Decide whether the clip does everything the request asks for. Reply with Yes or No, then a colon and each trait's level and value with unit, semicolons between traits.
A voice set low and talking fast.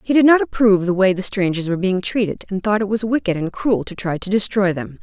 No: high, 200 Hz; fast, 275 wpm